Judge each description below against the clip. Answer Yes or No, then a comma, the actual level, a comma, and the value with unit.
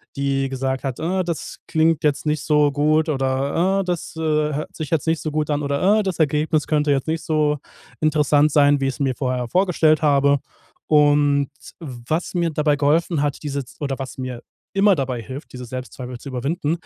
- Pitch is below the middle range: No, medium, 150 Hz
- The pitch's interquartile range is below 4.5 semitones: Yes, narrow, 2.5 semitones